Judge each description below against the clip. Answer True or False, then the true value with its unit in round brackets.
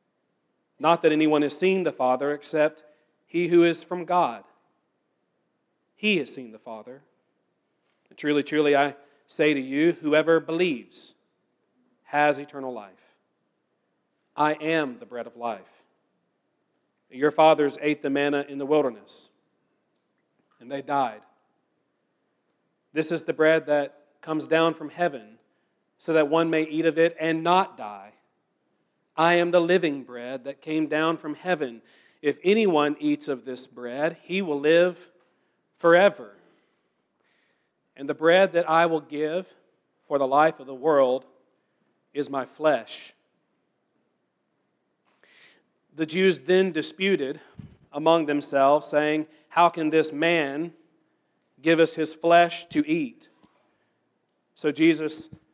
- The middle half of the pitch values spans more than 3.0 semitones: False (2.5 semitones)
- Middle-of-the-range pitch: True (155 Hz)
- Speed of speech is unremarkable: False (130 wpm)